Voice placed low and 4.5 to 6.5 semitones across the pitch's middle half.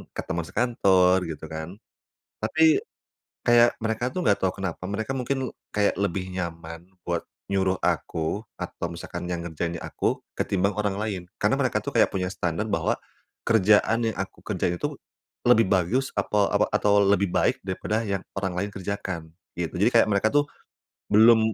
No: very low, 95 Hz; average, 3.5 semitones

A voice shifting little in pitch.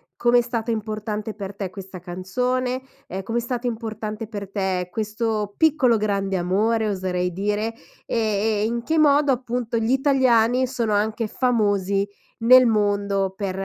No: average, 3.2 semitones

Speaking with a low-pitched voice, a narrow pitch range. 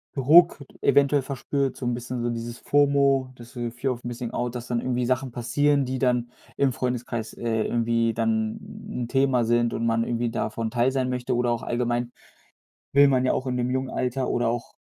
Yes: low, 125 Hz; narrow, 1.9 semitones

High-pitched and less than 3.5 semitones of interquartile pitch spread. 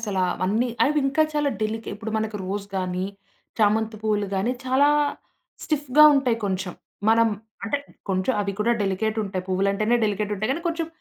No: high, 215 Hz; average, 4.0 semitones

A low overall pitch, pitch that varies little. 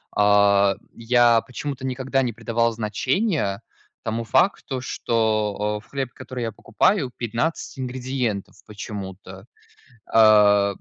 No: low, 115 Hz; average, 3.7 semitones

